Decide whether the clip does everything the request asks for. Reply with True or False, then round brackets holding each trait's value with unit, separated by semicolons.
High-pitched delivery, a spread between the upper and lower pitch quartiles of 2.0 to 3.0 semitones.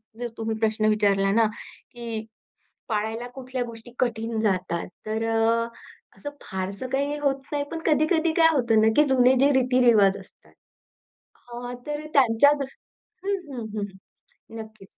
False (230 Hz; 3.5 semitones)